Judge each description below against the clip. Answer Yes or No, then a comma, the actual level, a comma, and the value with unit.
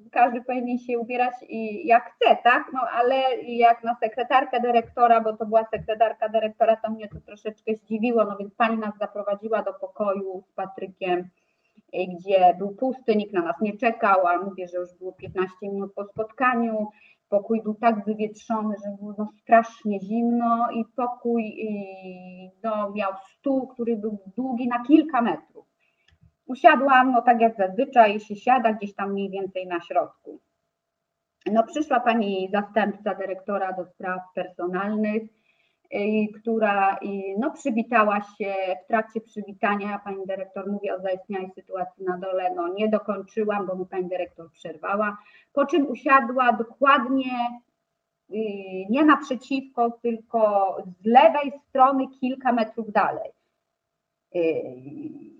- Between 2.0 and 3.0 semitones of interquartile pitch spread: No, average, 3.5 semitones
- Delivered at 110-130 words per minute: No, average, 140 wpm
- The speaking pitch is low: No, high, 215 Hz